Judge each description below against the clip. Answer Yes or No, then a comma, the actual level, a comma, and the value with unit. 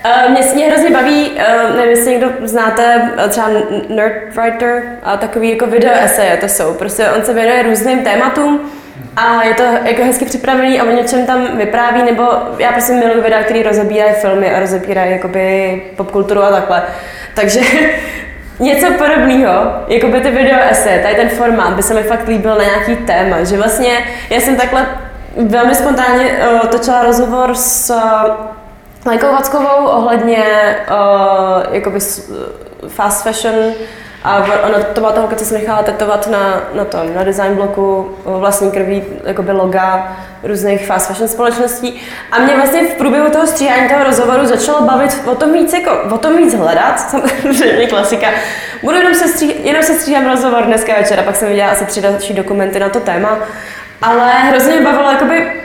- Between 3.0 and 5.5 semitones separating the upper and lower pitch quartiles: Yes, average, 3.9 semitones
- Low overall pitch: No, high, 230 Hz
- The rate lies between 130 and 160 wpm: No, fast, 170 wpm